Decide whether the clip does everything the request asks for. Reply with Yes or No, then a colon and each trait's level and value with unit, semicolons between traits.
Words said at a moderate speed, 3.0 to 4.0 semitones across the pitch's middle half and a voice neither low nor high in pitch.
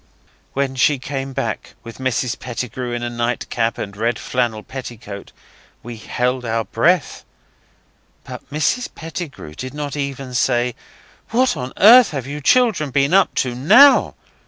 No: average, 145 wpm; average, 3.5 semitones; low, 130 Hz